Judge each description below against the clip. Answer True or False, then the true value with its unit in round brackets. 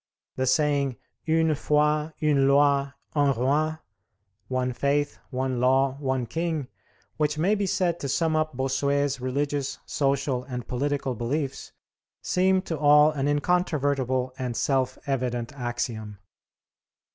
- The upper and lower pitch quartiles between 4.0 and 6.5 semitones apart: False (2.6 semitones)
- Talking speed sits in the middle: False (125 wpm)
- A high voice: False (140 Hz)